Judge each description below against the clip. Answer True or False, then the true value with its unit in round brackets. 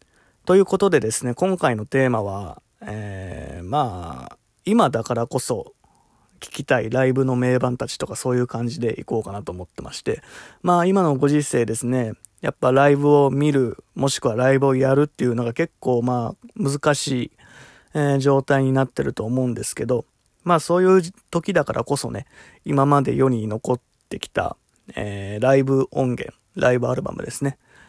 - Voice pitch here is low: True (130 Hz)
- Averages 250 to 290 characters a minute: False (340 characters per minute)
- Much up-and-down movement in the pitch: False (3.6 semitones)